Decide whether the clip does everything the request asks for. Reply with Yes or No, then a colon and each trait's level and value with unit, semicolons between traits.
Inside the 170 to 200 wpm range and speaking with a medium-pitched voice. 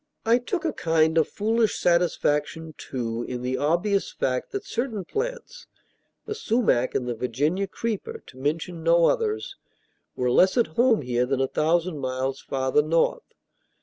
No: average, 155 wpm; medium, 165 Hz